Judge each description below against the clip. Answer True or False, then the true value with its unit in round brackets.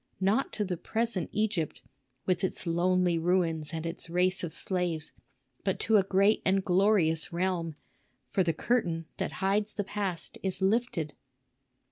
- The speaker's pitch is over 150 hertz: True (185 Hz)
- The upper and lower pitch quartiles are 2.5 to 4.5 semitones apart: True (3.0 semitones)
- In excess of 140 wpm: True (150 wpm)